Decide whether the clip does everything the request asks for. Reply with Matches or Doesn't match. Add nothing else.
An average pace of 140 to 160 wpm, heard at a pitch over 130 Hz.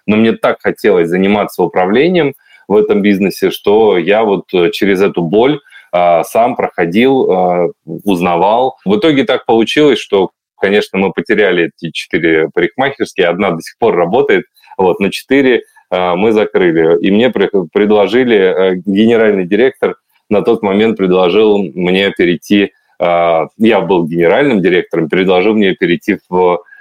Doesn't match